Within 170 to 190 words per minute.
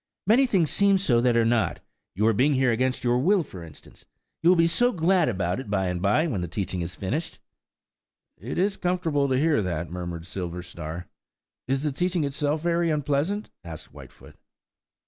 Yes: average, 180 wpm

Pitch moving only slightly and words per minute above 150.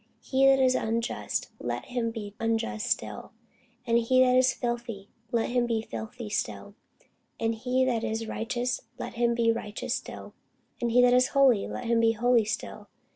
Yes: narrow, 1.8 semitones; average, 180 wpm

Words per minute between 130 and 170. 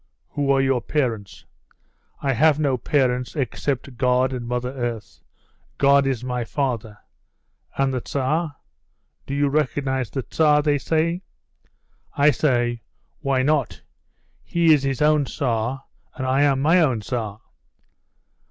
Yes: slow, 135 wpm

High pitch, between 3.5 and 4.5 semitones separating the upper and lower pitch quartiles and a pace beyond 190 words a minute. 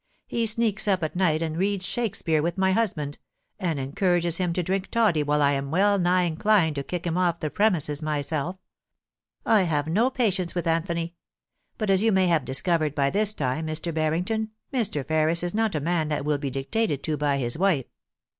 No: medium, 170 Hz; average, 4.2 semitones; average, 200 wpm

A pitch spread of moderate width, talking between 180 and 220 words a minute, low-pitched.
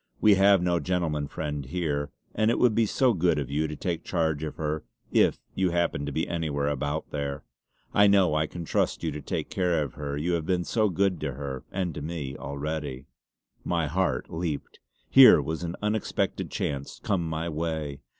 Yes: average, 3.6 semitones; average, 200 wpm; very low, 80 Hz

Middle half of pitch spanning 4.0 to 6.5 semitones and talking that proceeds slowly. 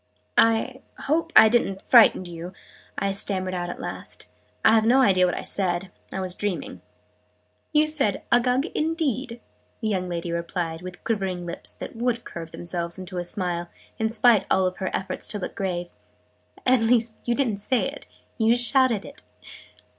No: average, 5.0 semitones; average, 170 wpm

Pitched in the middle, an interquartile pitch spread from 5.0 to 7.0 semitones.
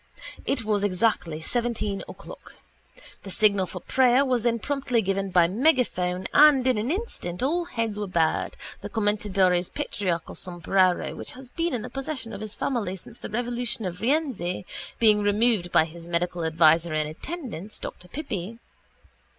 No: high, 210 Hz; wide, 5.6 semitones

